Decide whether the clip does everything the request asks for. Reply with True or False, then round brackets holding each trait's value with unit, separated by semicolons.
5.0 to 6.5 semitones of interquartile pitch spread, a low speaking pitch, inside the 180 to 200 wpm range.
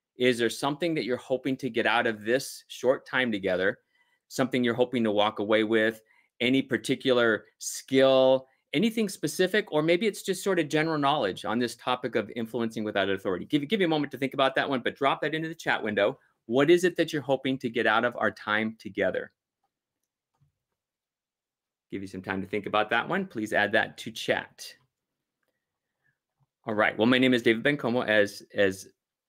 True (5.6 semitones; 130 Hz; 195 wpm)